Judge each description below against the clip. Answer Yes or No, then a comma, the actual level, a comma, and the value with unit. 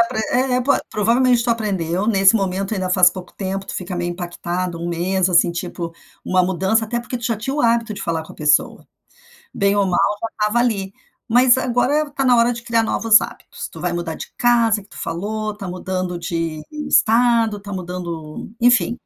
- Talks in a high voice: Yes, high, 200 Hz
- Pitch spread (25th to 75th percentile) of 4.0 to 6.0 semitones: Yes, average, 4.6 semitones